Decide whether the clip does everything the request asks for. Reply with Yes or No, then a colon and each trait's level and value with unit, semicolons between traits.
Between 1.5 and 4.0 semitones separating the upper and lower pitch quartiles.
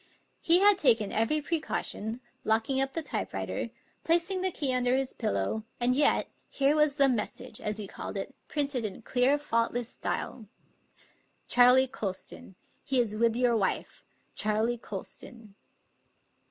No: average, 4.4 semitones